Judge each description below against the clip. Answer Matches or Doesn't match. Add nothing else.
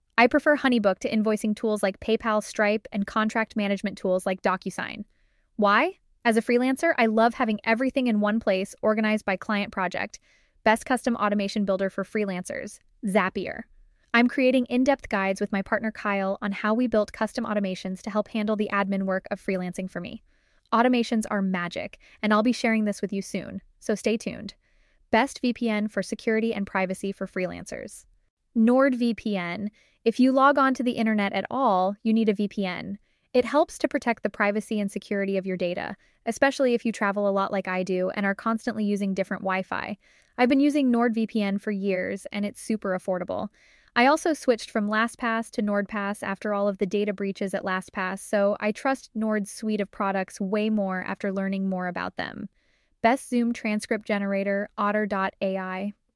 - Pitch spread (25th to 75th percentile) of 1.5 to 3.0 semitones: Matches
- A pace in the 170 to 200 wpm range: Matches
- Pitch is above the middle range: Matches